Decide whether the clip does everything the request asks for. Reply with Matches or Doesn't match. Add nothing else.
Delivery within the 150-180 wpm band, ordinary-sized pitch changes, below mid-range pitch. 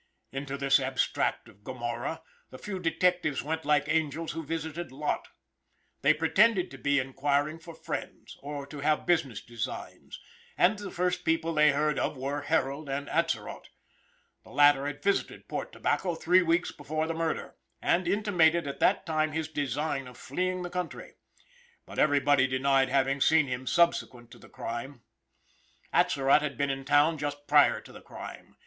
Doesn't match